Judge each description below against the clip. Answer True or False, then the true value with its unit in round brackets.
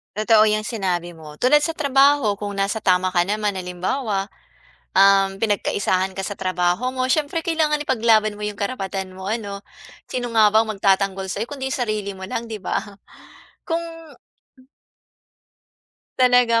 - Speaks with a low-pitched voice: False (210 Hz)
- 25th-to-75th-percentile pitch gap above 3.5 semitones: True (4.5 semitones)